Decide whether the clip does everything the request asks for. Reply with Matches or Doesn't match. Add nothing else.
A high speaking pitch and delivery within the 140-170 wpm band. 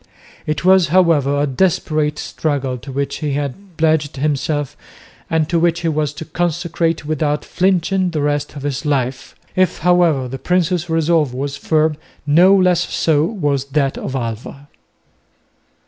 Doesn't match